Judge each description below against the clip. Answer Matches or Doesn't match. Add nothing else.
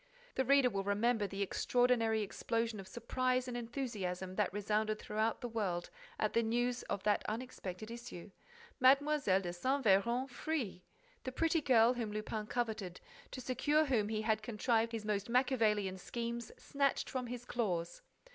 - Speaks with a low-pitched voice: Doesn't match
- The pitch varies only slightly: Doesn't match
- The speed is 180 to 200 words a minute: Doesn't match